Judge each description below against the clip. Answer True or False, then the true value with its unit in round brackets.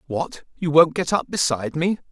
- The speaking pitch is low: False (155 Hz)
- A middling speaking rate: True (170 wpm)